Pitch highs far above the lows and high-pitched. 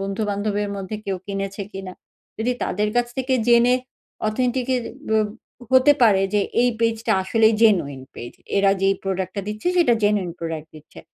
No: average, 3.4 semitones; high, 210 Hz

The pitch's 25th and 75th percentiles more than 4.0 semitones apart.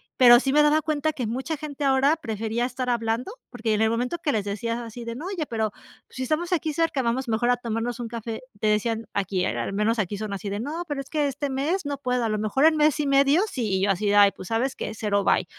Yes: average, 4.7 semitones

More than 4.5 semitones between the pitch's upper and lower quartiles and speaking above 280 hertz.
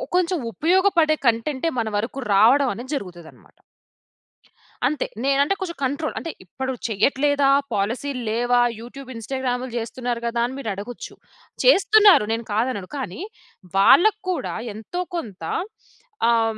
No: average, 5.1 semitones; very high, 255 Hz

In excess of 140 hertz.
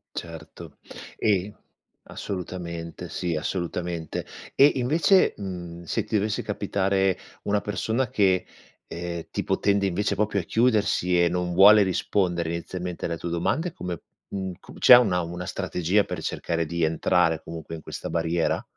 No: very low, 90 Hz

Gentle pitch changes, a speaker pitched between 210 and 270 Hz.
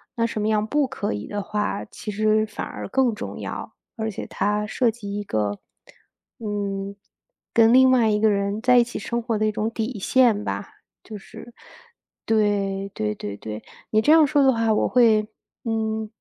Yes: narrow, 2.2 semitones; high, 215 Hz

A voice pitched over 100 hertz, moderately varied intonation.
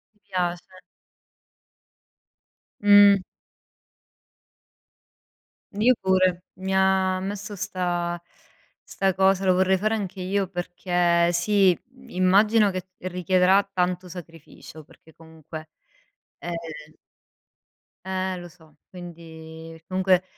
No: medium, 185 Hz; narrow, 1.8 semitones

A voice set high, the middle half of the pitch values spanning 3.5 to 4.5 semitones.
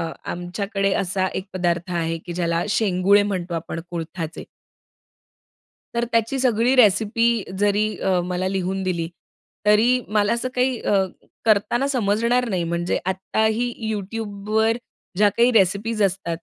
Yes: high, 200 Hz; average, 3.8 semitones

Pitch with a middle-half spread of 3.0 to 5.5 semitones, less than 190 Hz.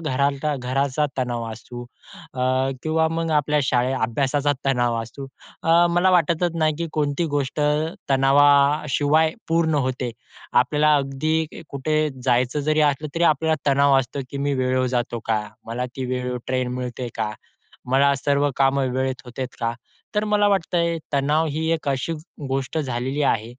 Yes: average, 3.4 semitones; medium, 140 Hz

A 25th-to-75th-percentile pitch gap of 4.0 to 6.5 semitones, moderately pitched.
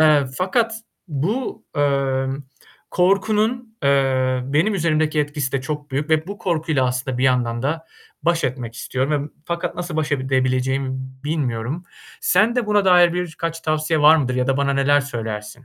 Yes: average, 4.4 semitones; medium, 145 Hz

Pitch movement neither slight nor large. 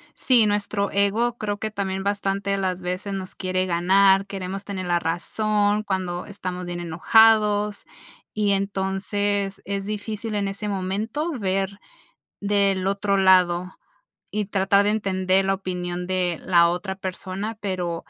No: narrow, 1.7 semitones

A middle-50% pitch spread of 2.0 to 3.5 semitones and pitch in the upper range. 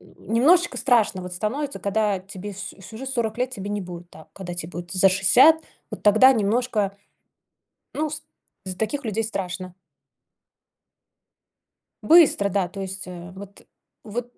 No: average, 4.8 semitones; high, 205 Hz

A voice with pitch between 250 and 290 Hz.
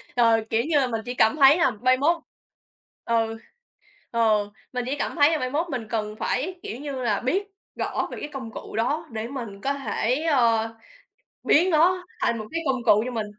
Yes: very high, 255 Hz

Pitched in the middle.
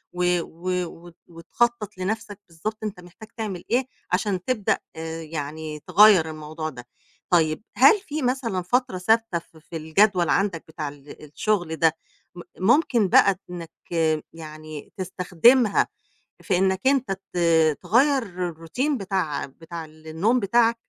Yes: medium, 180 Hz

